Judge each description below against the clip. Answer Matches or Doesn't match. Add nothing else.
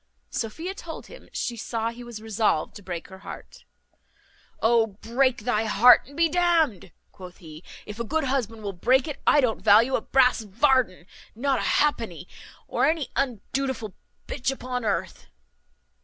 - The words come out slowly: Doesn't match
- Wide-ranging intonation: Doesn't match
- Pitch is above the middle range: Matches